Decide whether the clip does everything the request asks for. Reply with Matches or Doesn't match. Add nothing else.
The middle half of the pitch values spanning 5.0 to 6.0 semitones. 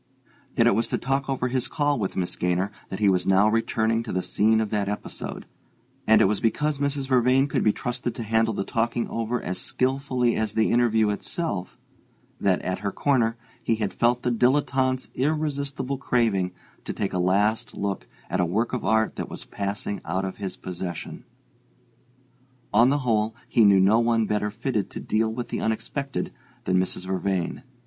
Doesn't match